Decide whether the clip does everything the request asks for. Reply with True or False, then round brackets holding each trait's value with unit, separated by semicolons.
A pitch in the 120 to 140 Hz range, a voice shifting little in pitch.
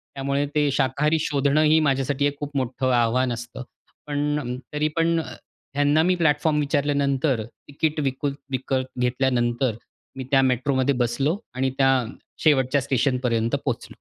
True (135 Hz; 2.3 semitones)